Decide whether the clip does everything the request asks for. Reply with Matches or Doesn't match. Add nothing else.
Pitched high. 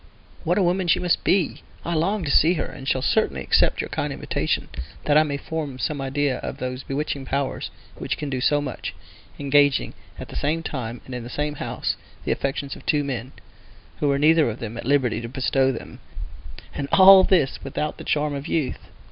Doesn't match